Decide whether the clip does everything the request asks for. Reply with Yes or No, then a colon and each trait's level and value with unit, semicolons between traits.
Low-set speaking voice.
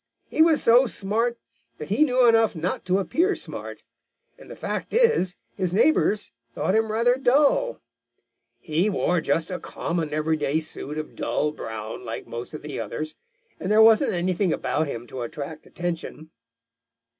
No: medium, 185 Hz